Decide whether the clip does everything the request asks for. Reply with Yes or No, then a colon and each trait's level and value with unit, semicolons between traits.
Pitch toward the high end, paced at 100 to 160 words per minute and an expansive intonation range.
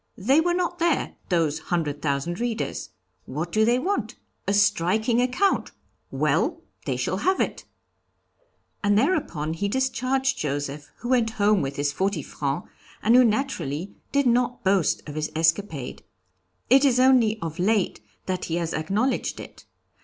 Yes: high, 205 Hz; average, 155 wpm; wide, 7.8 semitones